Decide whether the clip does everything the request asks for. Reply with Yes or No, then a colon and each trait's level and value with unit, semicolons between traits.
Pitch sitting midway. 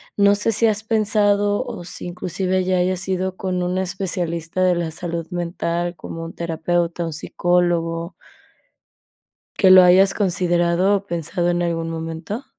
Yes: medium, 180 Hz